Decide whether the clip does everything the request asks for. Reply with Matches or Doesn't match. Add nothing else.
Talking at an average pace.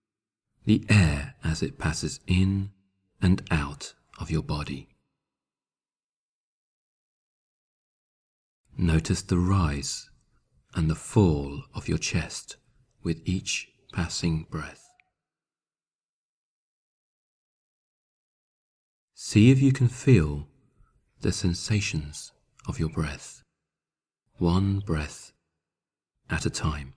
Doesn't match